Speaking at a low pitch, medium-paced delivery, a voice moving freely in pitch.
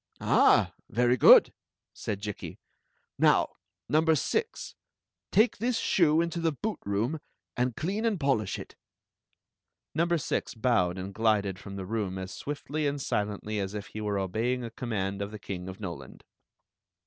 Yes: low, 110 Hz; average, 150 wpm; wide, 7.4 semitones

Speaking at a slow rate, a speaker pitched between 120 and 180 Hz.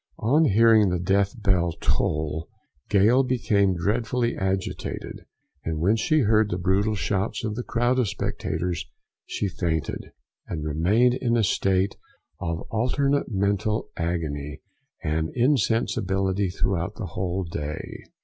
No: slow, 130 wpm; low, 100 Hz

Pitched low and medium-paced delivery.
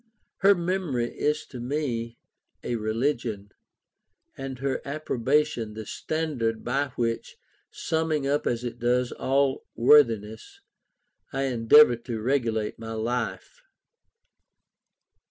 No: low, 125 Hz; slow, 105 wpm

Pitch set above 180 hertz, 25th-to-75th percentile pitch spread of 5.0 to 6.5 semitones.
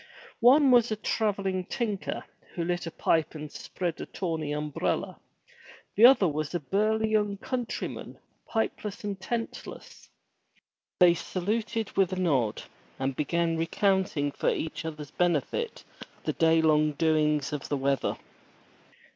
No: medium, 175 Hz; wide, 5.5 semitones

